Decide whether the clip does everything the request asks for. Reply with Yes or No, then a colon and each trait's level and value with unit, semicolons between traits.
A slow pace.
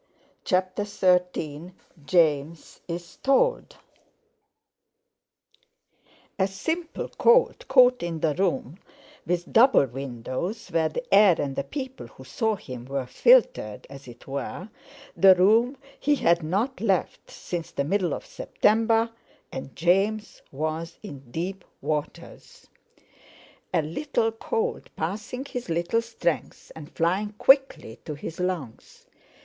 Yes: slow, 120 wpm